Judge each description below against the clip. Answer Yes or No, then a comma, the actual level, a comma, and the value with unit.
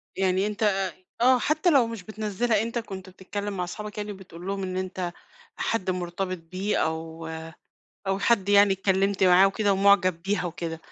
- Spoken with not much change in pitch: Yes, narrow, 2.2 semitones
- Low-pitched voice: No, high, 195 Hz